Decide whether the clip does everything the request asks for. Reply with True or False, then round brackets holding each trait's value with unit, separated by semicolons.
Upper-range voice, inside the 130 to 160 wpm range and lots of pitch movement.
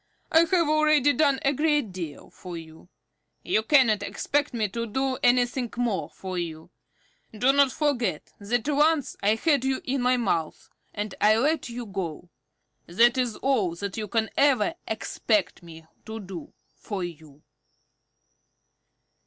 True (230 Hz; 150 wpm; 6.3 semitones)